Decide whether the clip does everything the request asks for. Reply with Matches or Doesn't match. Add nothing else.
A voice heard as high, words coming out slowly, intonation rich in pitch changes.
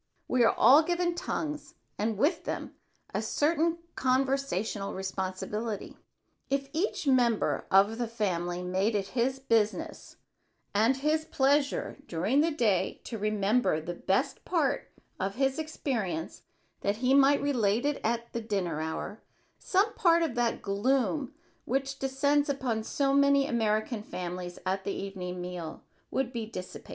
Doesn't match